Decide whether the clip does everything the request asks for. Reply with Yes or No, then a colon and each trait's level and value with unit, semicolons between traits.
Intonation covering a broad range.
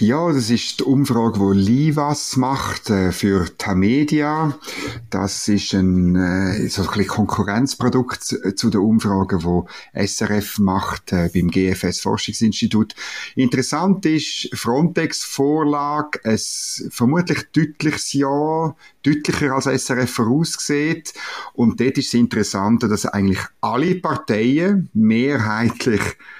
Yes: wide, 6.5 semitones